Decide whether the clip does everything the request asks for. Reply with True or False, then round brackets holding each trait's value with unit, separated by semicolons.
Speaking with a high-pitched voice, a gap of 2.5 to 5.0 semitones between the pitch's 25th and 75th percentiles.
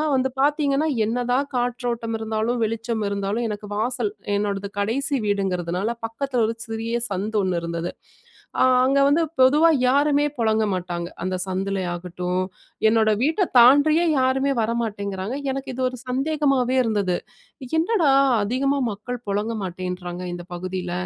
False (225 Hz; 5.4 semitones)